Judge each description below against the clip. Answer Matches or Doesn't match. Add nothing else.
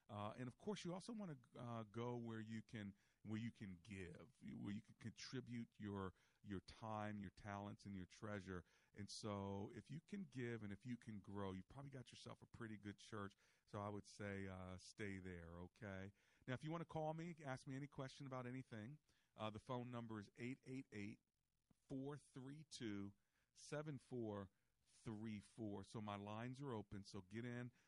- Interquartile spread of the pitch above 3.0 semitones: Matches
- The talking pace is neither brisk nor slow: Matches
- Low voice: Matches